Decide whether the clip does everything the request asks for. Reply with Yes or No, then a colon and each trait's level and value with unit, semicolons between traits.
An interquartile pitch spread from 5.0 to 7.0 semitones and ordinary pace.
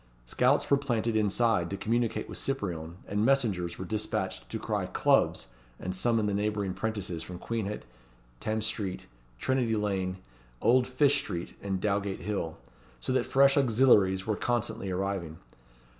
No: average, 4.1 semitones; average, 145 wpm